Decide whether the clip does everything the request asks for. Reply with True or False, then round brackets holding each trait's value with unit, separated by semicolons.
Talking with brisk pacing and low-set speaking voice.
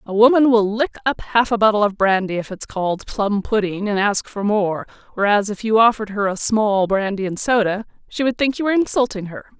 False (225 wpm; 210 Hz)